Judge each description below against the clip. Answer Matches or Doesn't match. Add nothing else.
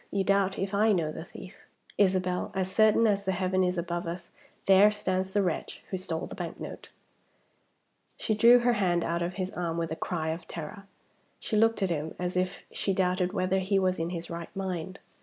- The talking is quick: Matches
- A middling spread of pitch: Doesn't match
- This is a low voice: Doesn't match